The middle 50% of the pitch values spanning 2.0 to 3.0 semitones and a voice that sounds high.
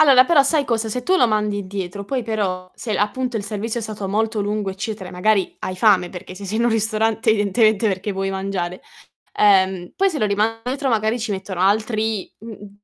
Yes: narrow, 2.6 semitones; high, 215 Hz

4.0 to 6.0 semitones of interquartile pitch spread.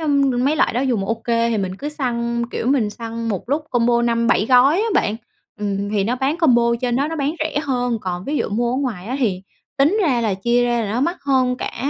No: average, 3.2 semitones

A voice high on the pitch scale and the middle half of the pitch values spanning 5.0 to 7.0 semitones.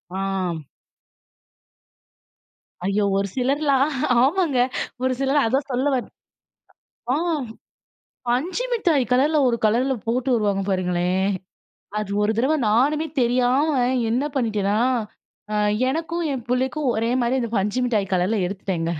Yes: high, 245 Hz; average, 5.3 semitones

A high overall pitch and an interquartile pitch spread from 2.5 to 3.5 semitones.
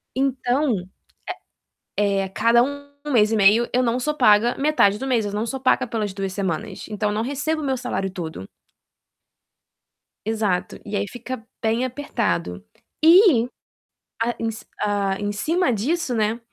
No: high, 230 Hz; average, 4.2 semitones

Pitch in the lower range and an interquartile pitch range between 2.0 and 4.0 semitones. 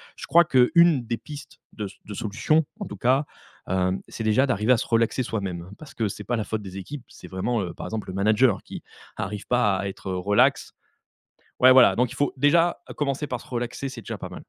No: low, 115 Hz; average, 4.7 semitones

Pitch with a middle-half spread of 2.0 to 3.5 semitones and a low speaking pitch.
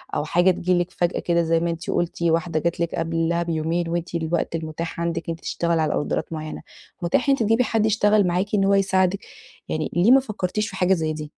No: narrow, 2.5 semitones; medium, 170 Hz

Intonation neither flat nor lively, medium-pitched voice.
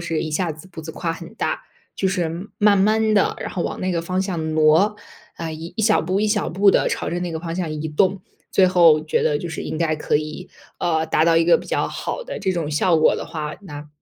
Yes: average, 3.1 semitones; medium, 170 Hz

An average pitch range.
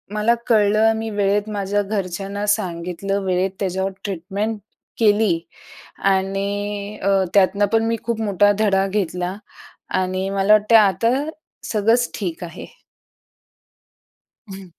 No: narrow, 1.8 semitones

